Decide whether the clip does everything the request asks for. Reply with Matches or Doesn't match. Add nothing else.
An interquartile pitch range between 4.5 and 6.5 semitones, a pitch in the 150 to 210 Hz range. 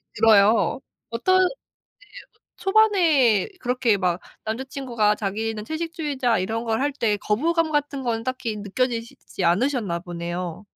Doesn't match